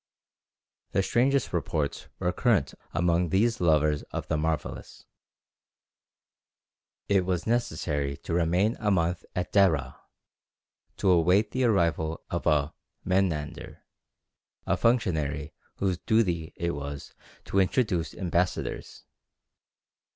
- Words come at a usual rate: No, slow, 105 wpm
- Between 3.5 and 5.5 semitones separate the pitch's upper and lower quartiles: Yes, average, 3.8 semitones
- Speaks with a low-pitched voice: Yes, very low, 85 Hz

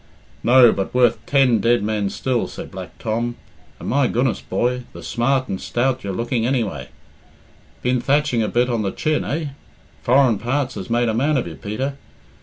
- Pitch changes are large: No, average, 2.9 semitones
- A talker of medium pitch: No, low, 120 Hz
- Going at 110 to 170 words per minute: No, average, 185 wpm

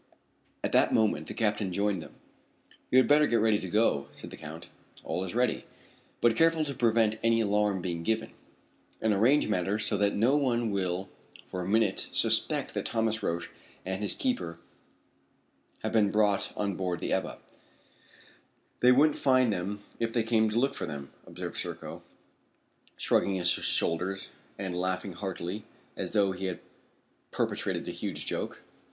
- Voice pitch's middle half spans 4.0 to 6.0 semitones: No, average, 3.6 semitones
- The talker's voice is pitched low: Yes, low, 105 Hz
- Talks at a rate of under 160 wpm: No, average, 165 wpm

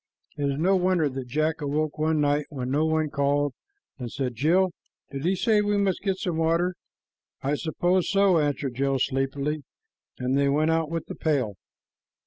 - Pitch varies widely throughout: No, average, 3.6 semitones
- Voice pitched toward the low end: No, medium, 155 Hz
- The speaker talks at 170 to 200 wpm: Yes, average, 180 wpm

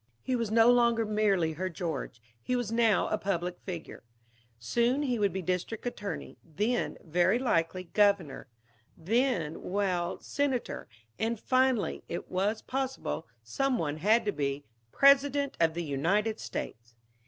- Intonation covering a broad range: Yes, wide, 5.9 semitones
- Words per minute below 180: Yes, average, 140 wpm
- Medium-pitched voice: No, high, 205 Hz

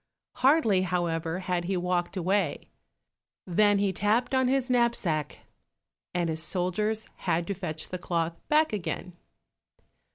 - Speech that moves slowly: Yes, slow, 130 wpm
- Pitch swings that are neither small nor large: Yes, average, 3.7 semitones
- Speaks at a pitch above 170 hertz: Yes, medium, 185 Hz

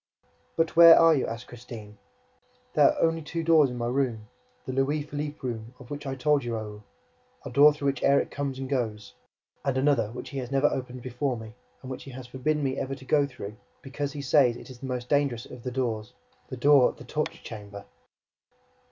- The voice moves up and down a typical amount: Yes, average, 3.0 semitones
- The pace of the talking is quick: Yes, fast, 215 wpm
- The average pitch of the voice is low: Yes, low, 130 Hz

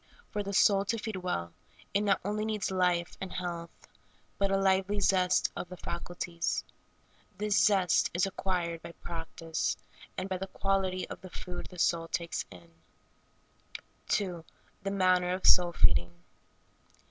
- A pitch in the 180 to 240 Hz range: Yes, medium, 185 Hz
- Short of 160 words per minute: Yes, average, 145 wpm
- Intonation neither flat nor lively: No, narrow, 2.3 semitones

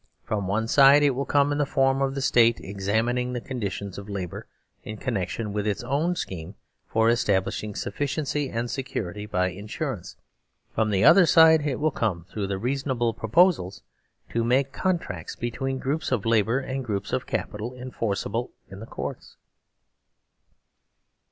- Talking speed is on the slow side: No, average, 160 wpm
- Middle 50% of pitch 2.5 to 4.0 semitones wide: No, average, 5.0 semitones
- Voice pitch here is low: Yes, low, 115 Hz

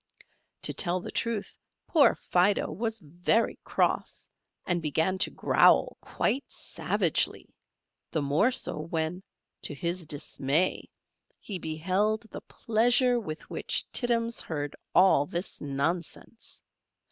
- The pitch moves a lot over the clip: Yes, wide, 5.9 semitones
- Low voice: No, medium, 180 Hz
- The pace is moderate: No, slow, 115 wpm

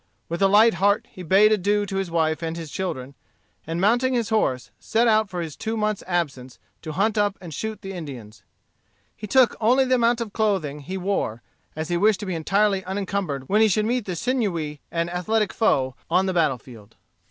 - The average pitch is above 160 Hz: Yes, high, 190 Hz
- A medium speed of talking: No, fast, 210 wpm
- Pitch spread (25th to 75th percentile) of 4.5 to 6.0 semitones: Yes, average, 4.9 semitones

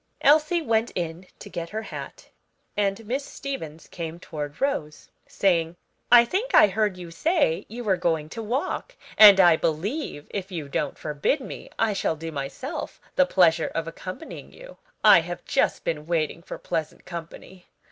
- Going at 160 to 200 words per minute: Yes, average, 165 wpm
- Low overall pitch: No, medium, 185 Hz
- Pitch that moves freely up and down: Yes, wide, 6.5 semitones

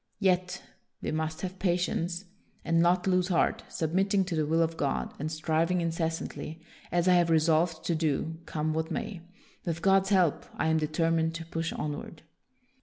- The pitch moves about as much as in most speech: No, narrow, 2.1 semitones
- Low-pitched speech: No, medium, 165 Hz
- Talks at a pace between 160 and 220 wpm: Yes, average, 175 wpm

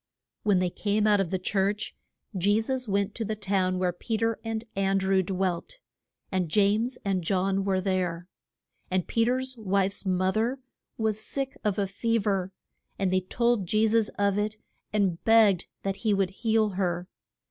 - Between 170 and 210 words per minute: Yes, average, 180 wpm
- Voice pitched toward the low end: No, high, 200 Hz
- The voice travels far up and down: No, average, 2.7 semitones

